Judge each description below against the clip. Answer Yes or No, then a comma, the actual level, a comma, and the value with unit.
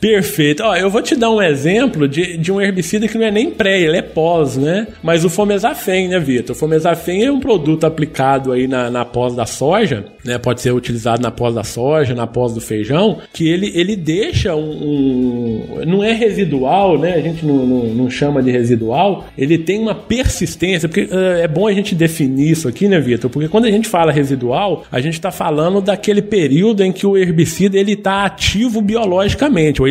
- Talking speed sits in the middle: No, fast, 210 wpm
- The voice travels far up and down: Yes, wide, 6.9 semitones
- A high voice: No, medium, 165 Hz